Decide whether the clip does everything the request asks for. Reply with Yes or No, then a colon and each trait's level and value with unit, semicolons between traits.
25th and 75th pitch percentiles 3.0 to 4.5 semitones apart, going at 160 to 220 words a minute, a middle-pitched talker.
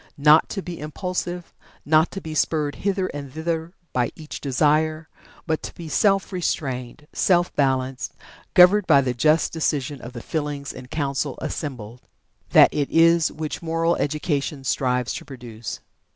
No: average, 3.6 semitones; average, 150 wpm; medium, 150 Hz